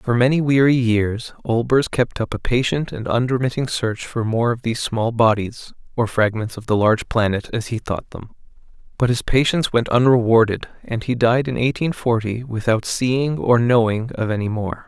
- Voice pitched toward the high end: No, low, 120 Hz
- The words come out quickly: No, average, 185 wpm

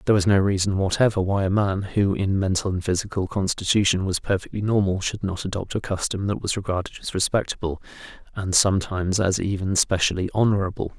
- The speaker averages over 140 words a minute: Yes, average, 180 wpm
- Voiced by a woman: No, male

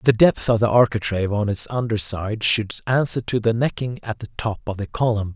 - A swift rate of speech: Yes, fast, 225 wpm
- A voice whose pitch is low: Yes, low, 110 Hz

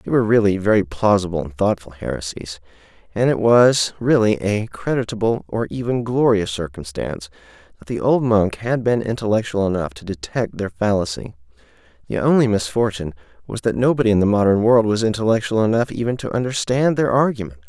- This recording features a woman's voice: No, male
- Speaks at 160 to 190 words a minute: Yes, average, 165 wpm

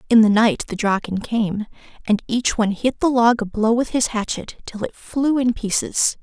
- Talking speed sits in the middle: No, fast, 210 wpm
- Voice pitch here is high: Yes, high, 225 Hz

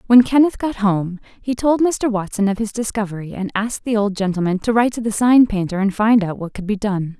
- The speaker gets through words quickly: Yes, fast, 240 wpm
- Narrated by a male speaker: No, female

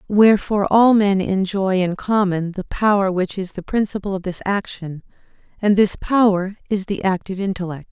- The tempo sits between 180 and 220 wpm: No, average, 165 wpm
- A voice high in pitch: Yes, high, 195 Hz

